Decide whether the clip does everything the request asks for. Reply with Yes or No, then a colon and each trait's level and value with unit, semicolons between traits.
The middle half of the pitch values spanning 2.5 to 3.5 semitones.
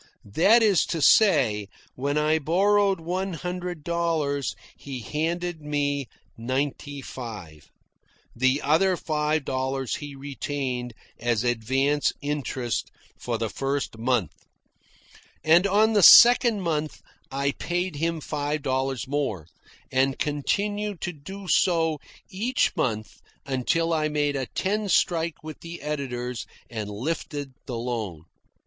No: average, 4.5 semitones